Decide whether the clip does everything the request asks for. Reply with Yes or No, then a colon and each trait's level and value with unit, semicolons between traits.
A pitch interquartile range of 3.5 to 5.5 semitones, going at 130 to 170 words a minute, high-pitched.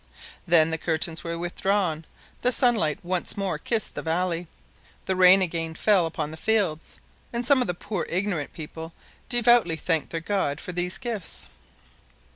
No: average, 3.9 semitones; average, 160 wpm; medium, 175 Hz